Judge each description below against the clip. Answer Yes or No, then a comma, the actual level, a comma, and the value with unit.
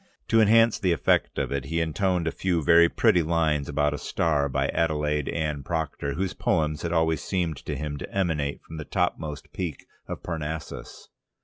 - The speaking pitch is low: Yes, very low, 80 Hz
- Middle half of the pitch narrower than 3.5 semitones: Yes, narrow, 2.5 semitones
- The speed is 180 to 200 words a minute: Yes, average, 185 wpm